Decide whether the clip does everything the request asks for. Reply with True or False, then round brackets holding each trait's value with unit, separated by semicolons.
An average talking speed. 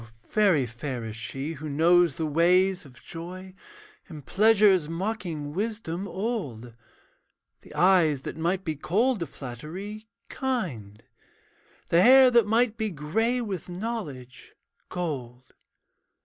False (120 wpm)